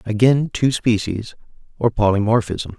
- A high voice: No, low, 110 Hz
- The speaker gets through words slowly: Yes, slow, 110 wpm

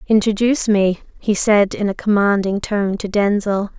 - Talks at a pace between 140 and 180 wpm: Yes, average, 160 wpm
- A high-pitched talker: Yes, high, 205 Hz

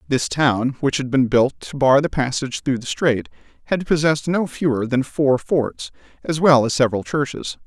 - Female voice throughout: No, male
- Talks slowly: No, average, 195 wpm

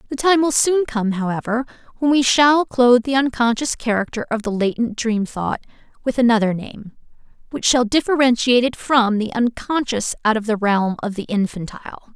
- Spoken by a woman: Yes, female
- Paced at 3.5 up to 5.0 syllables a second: No, 5.4 syllables/s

